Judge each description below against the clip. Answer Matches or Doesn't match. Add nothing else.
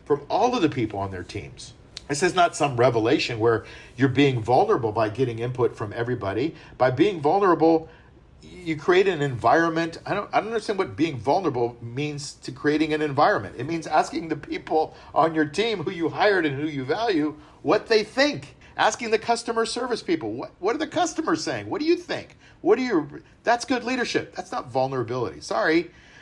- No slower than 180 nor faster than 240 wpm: Matches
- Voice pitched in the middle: Matches